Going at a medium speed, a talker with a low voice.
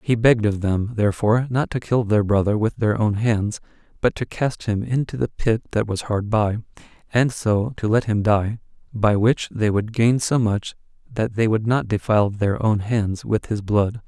No: fast, 210 wpm; low, 110 Hz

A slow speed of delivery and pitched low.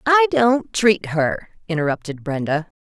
No: slow, 125 wpm; high, 190 Hz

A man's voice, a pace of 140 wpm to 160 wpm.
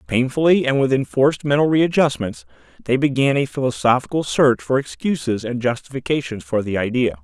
Yes: male; average, 150 wpm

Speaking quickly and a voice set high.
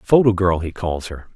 No: fast, 220 wpm; very low, 95 Hz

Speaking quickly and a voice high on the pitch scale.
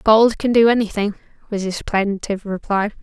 No: average, 160 wpm; high, 210 Hz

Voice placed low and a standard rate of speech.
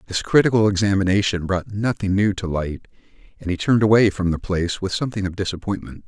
Yes: very low, 95 Hz; average, 190 wpm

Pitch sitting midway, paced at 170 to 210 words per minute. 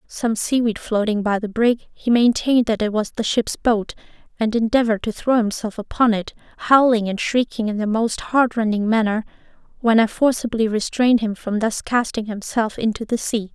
No: high, 225 Hz; average, 180 wpm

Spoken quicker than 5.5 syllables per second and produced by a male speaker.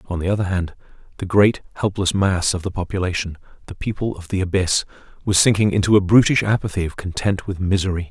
Yes: 6.1 syllables/s; male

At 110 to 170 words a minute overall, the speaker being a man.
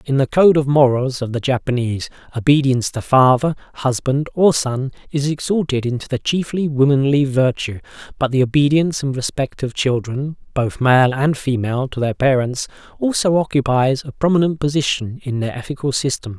Yes: average, 160 wpm; male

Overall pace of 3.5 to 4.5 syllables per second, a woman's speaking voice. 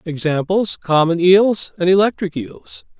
No: 4.1 syllables/s; male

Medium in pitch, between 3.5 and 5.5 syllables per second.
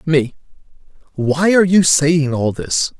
Yes: medium, 150 Hz; 3.9 syllables/s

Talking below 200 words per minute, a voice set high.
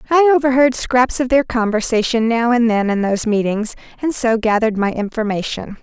Yes: average, 175 wpm; high, 230 Hz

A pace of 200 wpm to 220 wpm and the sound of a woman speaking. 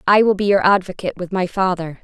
No: fast, 235 wpm; female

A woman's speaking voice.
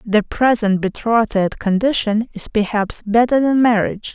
Yes: female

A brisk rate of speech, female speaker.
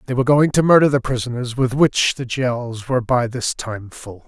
No: fast, 225 wpm; male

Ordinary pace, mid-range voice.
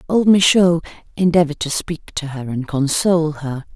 Yes: average, 160 wpm; medium, 160 Hz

